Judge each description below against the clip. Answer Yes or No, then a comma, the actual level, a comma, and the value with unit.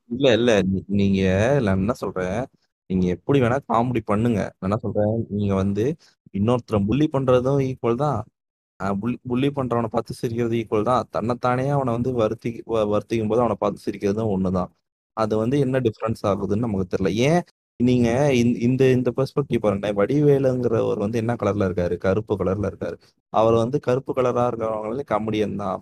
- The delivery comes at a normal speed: No, fast, 150 wpm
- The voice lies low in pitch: Yes, low, 115 Hz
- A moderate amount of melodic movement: Yes, average, 3.6 semitones